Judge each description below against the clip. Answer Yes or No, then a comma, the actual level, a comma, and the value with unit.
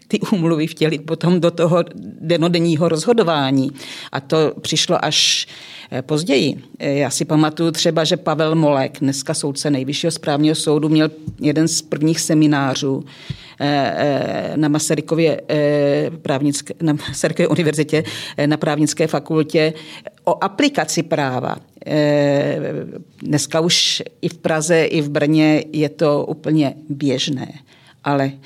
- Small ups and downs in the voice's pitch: Yes, narrow, 2.0 semitones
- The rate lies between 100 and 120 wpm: Yes, slow, 115 wpm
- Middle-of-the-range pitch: Yes, medium, 155 Hz